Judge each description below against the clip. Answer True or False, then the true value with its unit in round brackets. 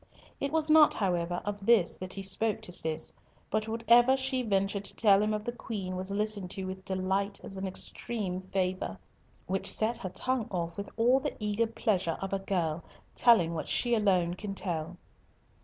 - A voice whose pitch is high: True (195 Hz)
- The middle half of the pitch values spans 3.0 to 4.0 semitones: True (3.5 semitones)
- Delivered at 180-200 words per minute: True (190 wpm)